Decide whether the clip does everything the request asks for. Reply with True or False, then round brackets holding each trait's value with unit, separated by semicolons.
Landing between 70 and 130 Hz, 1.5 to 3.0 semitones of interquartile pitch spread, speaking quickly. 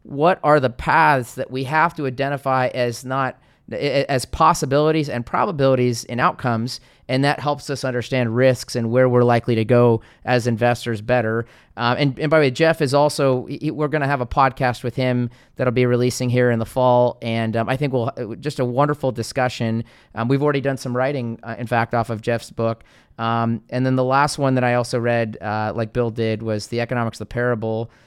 True (125 Hz; 2.6 semitones; 210 wpm)